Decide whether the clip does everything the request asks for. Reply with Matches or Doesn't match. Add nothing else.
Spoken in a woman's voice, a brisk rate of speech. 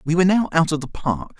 Doesn't match